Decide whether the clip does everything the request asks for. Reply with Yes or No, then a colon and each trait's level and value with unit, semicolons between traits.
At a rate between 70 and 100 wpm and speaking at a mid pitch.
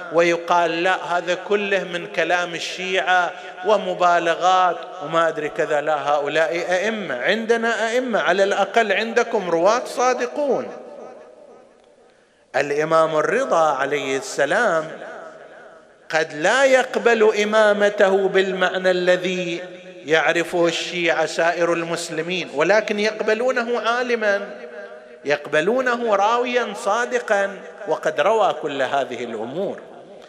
Yes: average, 90 wpm; medium, 180 Hz